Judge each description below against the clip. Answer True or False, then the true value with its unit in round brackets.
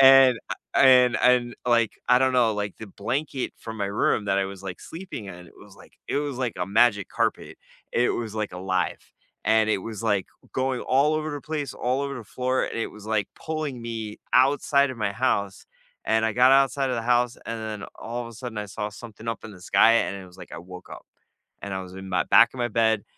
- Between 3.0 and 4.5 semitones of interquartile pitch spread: True (4.1 semitones)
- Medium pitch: False (115 Hz)